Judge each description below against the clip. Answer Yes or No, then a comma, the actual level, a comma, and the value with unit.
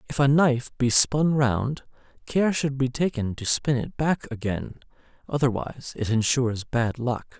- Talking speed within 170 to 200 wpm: No, average, 160 wpm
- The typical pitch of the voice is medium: No, low, 130 Hz